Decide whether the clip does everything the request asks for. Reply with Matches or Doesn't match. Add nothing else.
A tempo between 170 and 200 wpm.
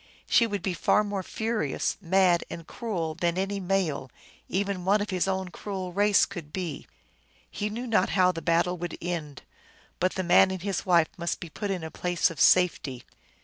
Matches